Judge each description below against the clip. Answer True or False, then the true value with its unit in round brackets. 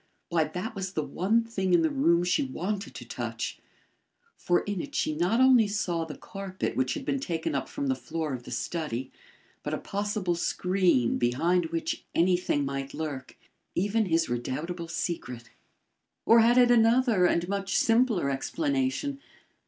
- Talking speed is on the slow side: False (165 wpm)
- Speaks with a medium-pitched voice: True (180 Hz)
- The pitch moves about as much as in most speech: False (5.8 semitones)